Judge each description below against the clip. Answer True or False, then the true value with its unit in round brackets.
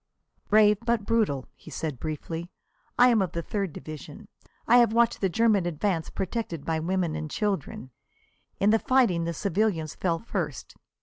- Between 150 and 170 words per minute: True (165 wpm)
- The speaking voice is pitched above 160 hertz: True (185 Hz)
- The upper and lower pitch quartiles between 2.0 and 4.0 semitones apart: False (5.2 semitones)